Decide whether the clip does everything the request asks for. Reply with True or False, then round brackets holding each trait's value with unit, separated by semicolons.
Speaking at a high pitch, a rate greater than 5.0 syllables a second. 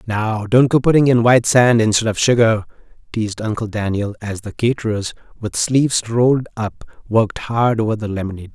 False (110 Hz; 5.6 syllables/s)